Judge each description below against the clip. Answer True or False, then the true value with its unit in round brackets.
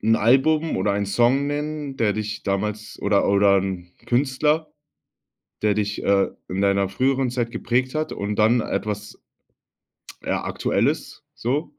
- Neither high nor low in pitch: False (110 Hz)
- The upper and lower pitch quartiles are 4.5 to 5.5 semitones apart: True (4.9 semitones)